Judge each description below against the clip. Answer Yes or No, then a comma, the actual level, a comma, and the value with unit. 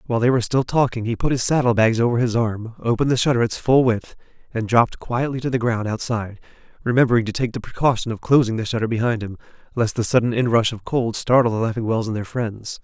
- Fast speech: Yes, fast, 230 wpm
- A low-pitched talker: Yes, low, 115 Hz